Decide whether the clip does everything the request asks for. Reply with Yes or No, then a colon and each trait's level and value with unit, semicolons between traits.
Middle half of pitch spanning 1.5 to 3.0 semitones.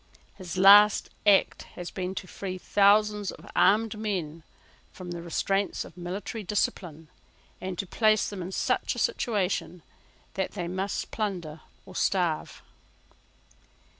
Yes: average, 2.7 semitones